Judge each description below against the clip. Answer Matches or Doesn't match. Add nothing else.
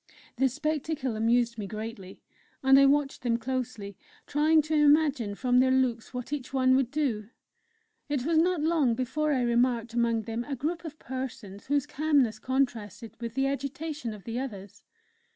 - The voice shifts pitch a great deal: Doesn't match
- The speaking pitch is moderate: Doesn't match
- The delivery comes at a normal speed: Matches